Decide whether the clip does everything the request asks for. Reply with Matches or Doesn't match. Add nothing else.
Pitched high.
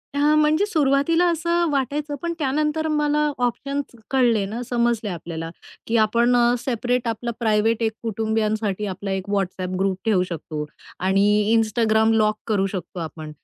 Matches